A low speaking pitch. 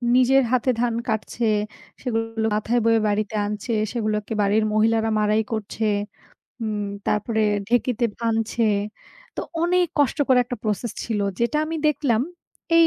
No: high, 225 Hz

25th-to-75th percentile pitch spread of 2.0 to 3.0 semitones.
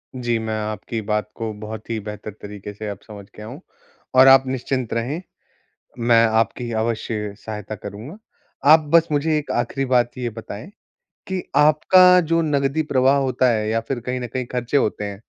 No: average, 4.0 semitones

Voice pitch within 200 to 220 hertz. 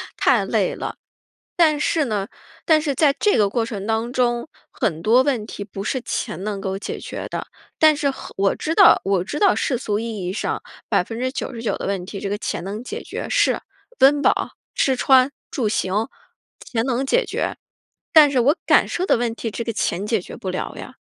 No: high, 235 Hz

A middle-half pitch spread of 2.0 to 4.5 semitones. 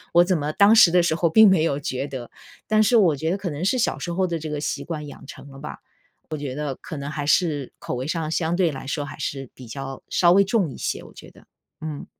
Yes: average, 4.1 semitones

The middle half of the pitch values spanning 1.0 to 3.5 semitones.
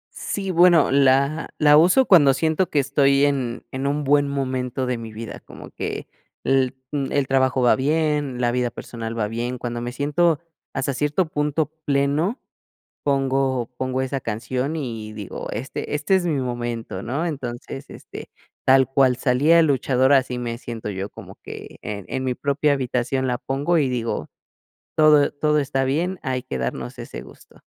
Yes: average, 3.1 semitones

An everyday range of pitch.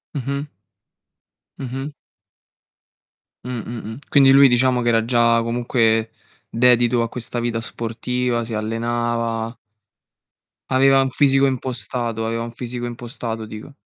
No: narrow, 1.8 semitones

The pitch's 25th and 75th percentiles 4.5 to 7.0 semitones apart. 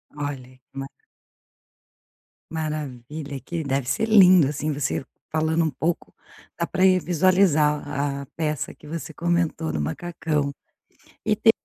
No: average, 3.2 semitones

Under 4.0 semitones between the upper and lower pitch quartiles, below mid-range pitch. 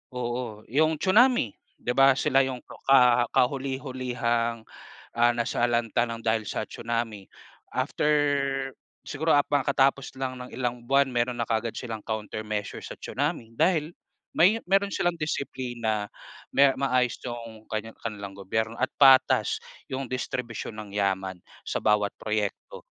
Yes: average, 3.4 semitones; low, 120 Hz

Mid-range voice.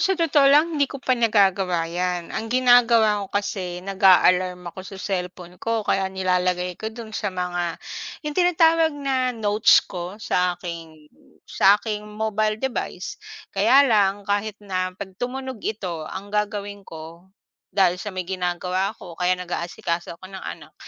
No: high, 195 Hz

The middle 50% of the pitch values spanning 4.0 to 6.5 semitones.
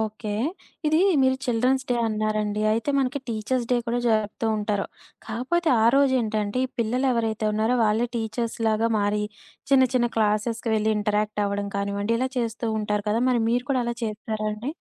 No: narrow, 2.5 semitones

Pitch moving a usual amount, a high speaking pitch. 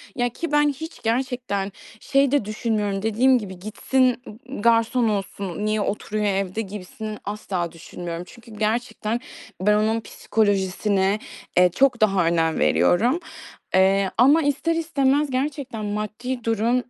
Yes: average, 4.3 semitones; high, 215 Hz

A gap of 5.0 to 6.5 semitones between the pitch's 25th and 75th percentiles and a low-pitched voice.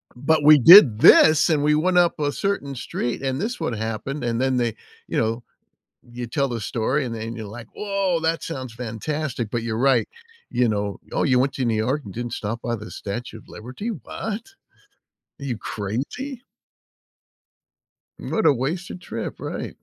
Yes: average, 5.3 semitones; low, 130 Hz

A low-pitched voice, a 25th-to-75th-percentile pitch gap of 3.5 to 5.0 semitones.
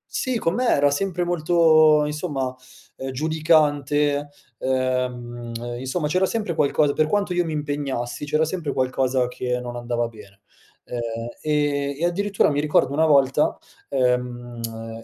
No: medium, 145 Hz; average, 4.1 semitones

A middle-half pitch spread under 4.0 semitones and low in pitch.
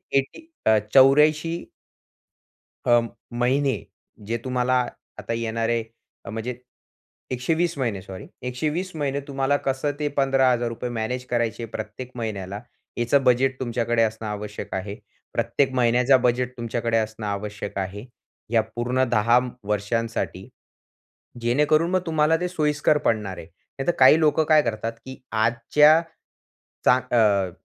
Yes: average, 3.4 semitones; low, 120 Hz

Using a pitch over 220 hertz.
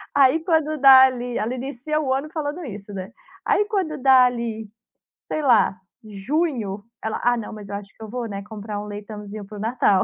Yes: high, 235 Hz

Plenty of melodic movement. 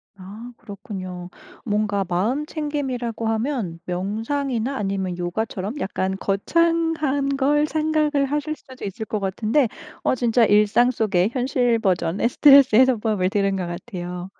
Yes: wide, 5.9 semitones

